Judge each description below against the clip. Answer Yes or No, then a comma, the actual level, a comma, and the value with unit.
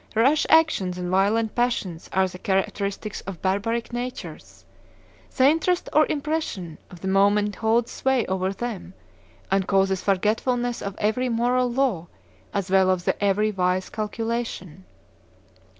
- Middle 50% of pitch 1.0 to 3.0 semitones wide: No, average, 4.2 semitones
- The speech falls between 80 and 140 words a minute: Yes, slow, 135 wpm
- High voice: Yes, high, 210 Hz